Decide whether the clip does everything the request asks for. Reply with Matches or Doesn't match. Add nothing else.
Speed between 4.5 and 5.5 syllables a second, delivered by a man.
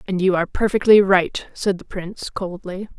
Doesn't match